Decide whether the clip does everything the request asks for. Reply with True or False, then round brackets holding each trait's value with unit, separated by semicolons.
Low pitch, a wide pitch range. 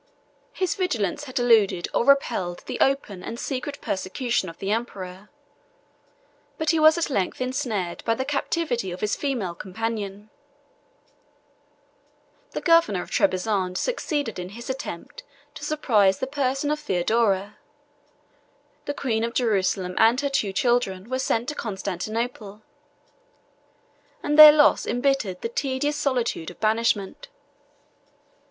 False (230 Hz; 6.0 semitones)